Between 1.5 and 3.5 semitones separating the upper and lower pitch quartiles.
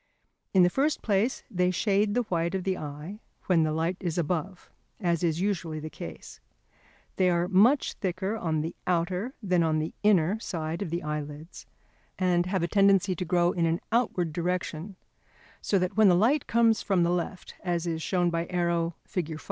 Yes: average, 2.8 semitones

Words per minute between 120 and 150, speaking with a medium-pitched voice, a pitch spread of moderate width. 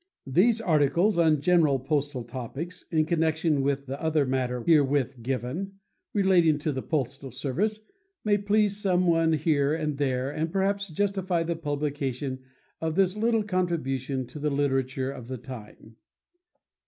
Yes: average, 140 wpm; medium, 150 Hz; average, 5.0 semitones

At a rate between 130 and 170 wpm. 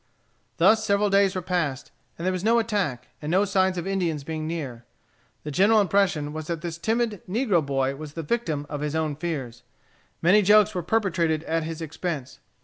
No: average, 190 wpm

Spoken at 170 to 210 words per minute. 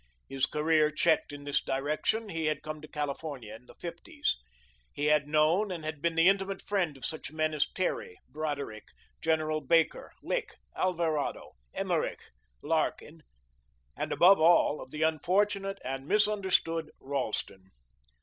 No: average, 145 wpm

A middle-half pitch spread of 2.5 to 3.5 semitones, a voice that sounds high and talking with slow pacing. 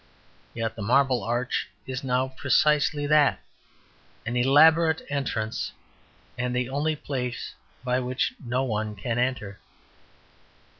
No: average, 2.8 semitones; low, 125 Hz; slow, 115 wpm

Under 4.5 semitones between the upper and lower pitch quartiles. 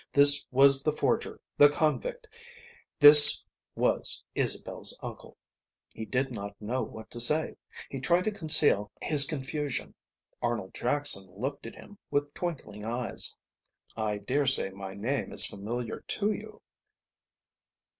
No: average, 5.1 semitones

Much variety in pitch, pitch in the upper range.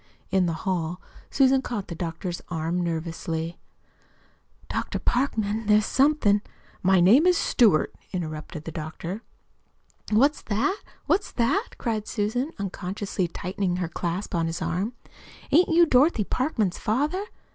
Yes: wide, 6.5 semitones; high, 200 Hz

